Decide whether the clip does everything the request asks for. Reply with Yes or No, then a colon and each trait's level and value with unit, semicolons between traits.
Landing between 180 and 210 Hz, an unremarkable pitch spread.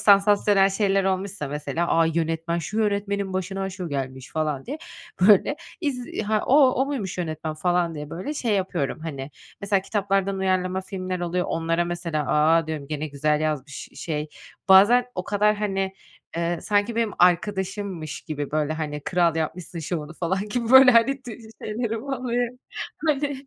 Yes: medium, 185 Hz; average, 4.5 semitones